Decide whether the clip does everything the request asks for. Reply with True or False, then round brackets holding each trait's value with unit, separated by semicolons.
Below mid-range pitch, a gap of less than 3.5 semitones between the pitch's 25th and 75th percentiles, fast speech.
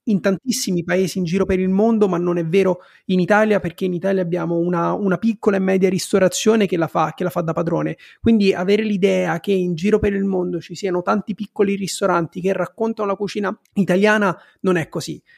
False (190 Hz; 2.6 semitones; 210 wpm)